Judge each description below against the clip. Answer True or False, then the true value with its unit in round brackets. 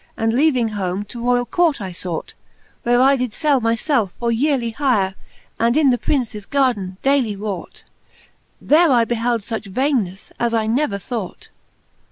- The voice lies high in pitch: True (235 Hz)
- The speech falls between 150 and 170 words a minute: True (165 wpm)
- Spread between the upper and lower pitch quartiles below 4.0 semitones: False (4.3 semitones)